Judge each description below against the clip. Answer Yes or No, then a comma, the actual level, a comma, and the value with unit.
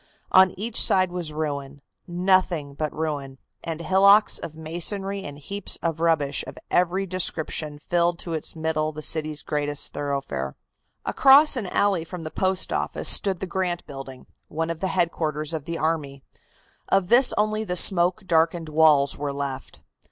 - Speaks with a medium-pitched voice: Yes, medium, 165 Hz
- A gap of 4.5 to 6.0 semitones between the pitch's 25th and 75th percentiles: No, average, 3.7 semitones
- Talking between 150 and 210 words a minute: Yes, average, 160 wpm